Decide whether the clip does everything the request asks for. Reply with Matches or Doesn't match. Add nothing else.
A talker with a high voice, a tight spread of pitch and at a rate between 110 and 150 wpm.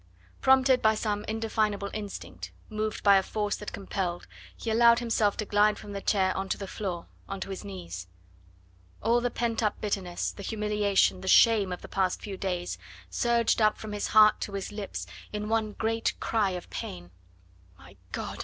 Doesn't match